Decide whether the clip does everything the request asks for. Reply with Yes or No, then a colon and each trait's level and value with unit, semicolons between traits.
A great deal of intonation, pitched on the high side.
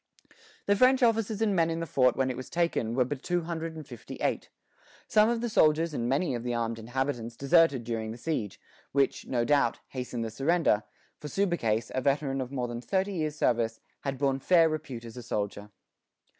No: wide, 5.7 semitones; low, 135 Hz